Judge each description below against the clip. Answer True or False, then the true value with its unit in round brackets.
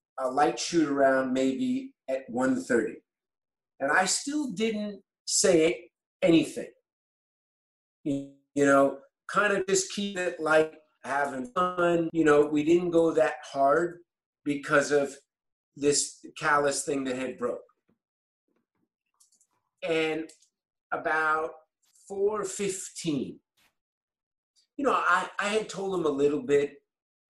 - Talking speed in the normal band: False (110 wpm)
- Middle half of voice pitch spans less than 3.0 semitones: False (4.9 semitones)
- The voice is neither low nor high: True (155 Hz)